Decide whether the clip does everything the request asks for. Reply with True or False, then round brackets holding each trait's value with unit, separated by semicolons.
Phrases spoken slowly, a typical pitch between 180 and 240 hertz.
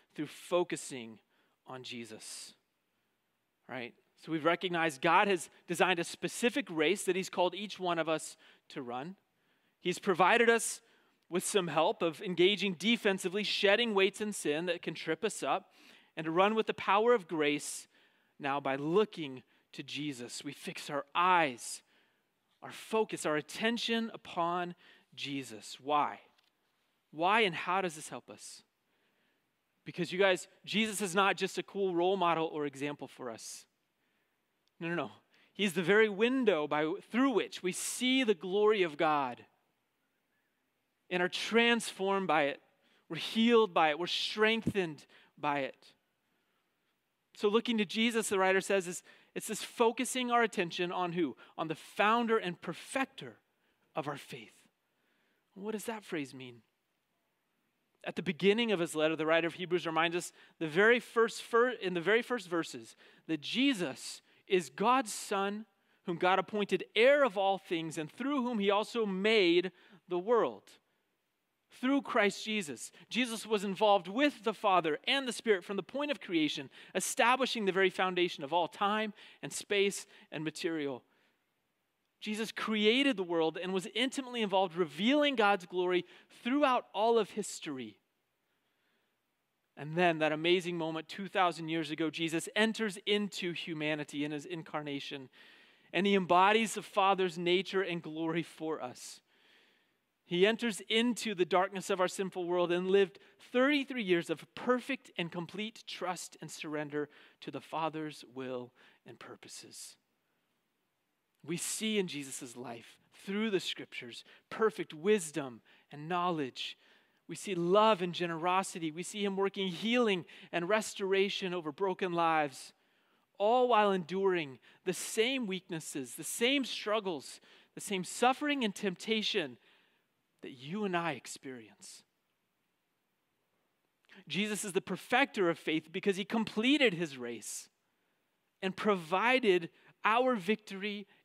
False (145 wpm; 190 Hz)